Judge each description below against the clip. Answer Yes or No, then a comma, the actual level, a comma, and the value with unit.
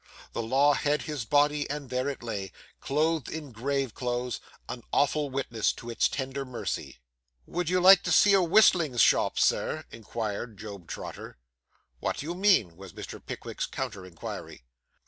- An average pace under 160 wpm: No, average, 165 wpm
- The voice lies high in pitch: No, low, 135 Hz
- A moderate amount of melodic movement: Yes, average, 4.7 semitones